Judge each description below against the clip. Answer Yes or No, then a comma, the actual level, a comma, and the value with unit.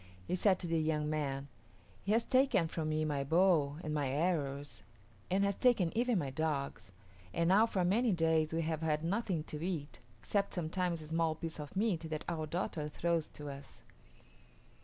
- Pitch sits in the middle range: Yes, medium, 160 Hz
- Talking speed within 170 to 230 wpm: Yes, average, 185 wpm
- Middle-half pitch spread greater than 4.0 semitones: No, average, 3.4 semitones